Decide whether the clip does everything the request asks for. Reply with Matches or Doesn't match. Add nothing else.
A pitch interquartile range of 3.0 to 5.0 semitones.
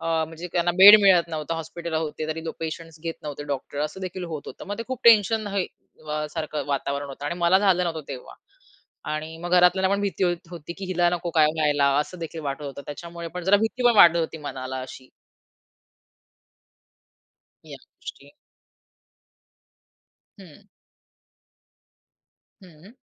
Matches